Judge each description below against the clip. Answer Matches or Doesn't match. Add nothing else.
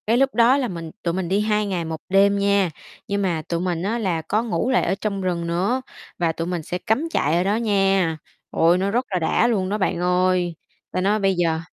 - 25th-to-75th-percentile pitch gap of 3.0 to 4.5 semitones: Matches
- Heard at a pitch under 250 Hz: Matches